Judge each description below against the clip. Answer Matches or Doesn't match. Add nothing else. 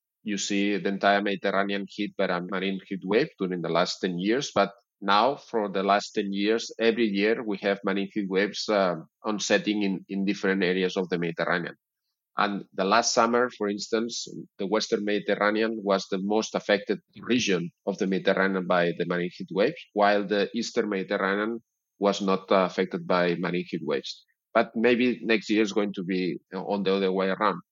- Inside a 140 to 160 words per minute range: Doesn't match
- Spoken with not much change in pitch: Matches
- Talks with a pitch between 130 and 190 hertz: Doesn't match